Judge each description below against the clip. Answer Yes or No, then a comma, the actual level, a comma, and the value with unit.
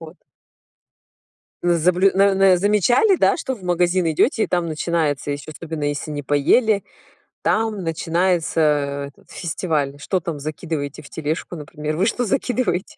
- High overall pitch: No, medium, 170 Hz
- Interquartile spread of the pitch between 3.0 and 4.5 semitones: Yes, average, 4.1 semitones